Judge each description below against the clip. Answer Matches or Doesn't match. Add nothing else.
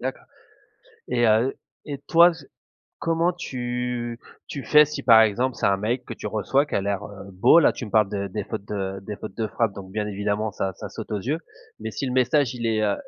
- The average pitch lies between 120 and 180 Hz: Doesn't match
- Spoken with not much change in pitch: Doesn't match